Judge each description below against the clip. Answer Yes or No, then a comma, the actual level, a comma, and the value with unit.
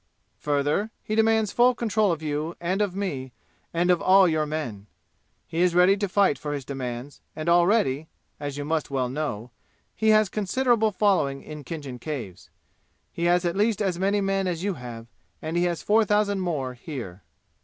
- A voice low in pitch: No, medium, 170 Hz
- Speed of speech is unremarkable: Yes, average, 185 wpm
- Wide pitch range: Yes, wide, 5.8 semitones